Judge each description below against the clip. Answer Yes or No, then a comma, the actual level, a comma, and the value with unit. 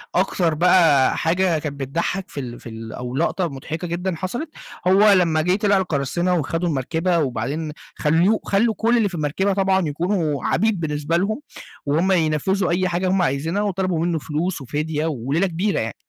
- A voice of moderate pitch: Yes, medium, 170 Hz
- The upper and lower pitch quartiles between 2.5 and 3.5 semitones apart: No, average, 4.1 semitones